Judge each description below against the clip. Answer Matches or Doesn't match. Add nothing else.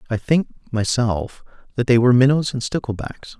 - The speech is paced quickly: Doesn't match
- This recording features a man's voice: Matches